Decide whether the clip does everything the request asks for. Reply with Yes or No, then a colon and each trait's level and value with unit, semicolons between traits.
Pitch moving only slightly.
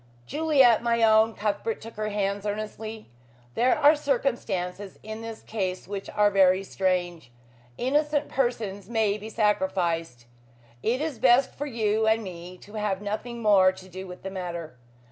No: average, 3.6 semitones